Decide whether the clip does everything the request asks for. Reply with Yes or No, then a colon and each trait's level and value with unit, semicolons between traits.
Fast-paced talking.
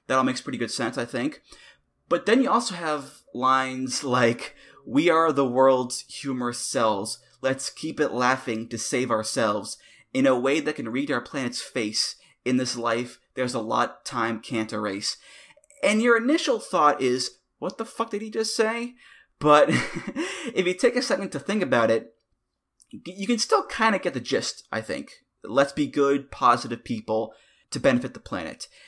No: average, 180 wpm